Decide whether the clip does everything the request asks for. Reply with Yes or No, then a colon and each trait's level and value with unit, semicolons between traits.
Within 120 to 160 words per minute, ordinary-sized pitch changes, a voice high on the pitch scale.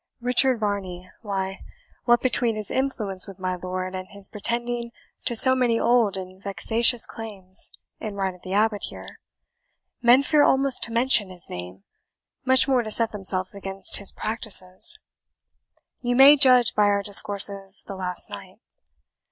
Yes: average, 155 wpm; average, 4.0 semitones; high, 210 Hz